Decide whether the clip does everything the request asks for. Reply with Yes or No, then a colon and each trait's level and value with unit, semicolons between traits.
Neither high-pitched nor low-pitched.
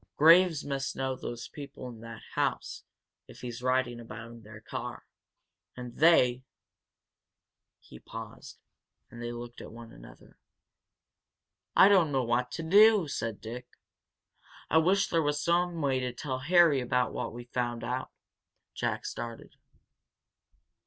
No: low, 125 Hz